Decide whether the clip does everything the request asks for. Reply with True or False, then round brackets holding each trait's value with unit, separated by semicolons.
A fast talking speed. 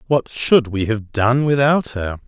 False (185 wpm)